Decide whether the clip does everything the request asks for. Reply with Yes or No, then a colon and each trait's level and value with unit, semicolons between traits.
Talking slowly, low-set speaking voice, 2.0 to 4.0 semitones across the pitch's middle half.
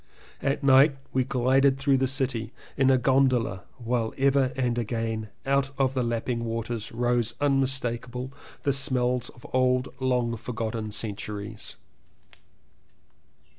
Yes: slow, 125 wpm; low, 125 Hz; narrow, 2.5 semitones